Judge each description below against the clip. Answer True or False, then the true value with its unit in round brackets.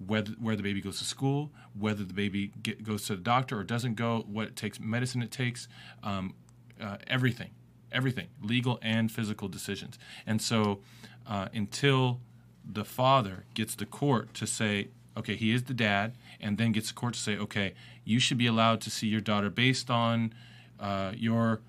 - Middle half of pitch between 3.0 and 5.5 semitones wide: False (2.6 semitones)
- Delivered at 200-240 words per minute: False (190 wpm)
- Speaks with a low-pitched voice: True (110 Hz)